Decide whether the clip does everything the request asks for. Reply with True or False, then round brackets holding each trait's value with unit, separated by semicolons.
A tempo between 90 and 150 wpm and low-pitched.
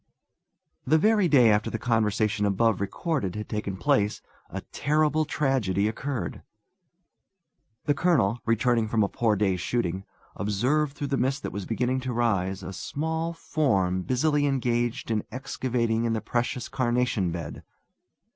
True (145 wpm; 120 Hz)